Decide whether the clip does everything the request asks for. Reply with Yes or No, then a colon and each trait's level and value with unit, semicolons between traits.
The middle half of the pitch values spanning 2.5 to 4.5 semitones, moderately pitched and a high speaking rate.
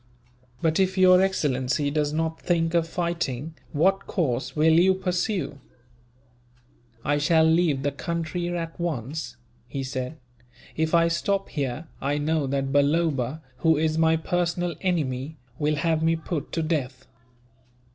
No: average, 3.1 semitones; medium, 160 Hz; average, 140 wpm